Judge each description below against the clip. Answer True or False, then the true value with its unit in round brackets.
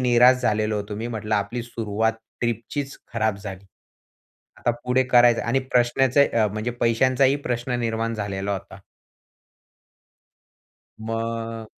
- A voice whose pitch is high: False (115 Hz)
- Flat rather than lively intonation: True (2.2 semitones)